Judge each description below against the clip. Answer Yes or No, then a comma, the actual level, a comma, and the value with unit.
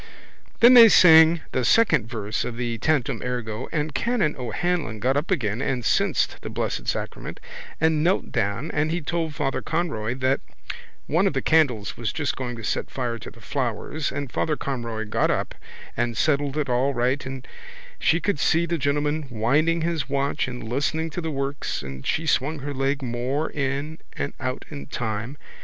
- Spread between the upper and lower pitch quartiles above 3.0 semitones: Yes, average, 4.4 semitones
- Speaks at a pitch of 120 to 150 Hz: Yes, medium, 140 Hz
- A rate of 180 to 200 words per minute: Yes, average, 185 wpm